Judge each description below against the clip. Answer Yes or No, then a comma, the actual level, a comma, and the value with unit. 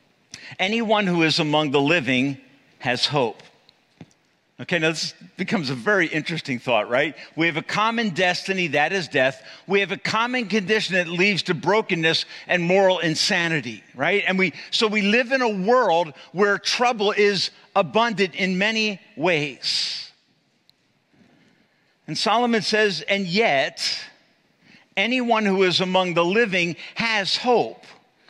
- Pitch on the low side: No, high, 190 Hz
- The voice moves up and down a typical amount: Yes, average, 4.4 semitones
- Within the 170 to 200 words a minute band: No, average, 140 wpm